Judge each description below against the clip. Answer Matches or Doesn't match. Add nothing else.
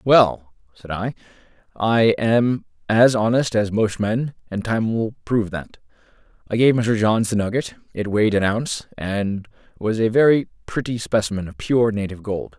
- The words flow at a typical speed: Matches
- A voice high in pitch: Doesn't match